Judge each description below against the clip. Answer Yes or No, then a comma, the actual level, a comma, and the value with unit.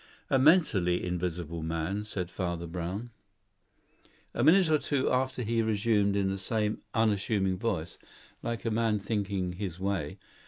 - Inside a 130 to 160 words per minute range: Yes, average, 145 wpm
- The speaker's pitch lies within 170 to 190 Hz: No, low, 100 Hz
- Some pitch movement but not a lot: Yes, average, 4.3 semitones